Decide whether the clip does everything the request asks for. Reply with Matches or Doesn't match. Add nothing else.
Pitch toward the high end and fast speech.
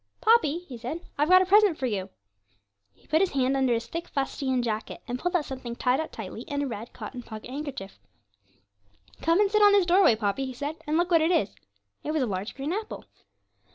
Matches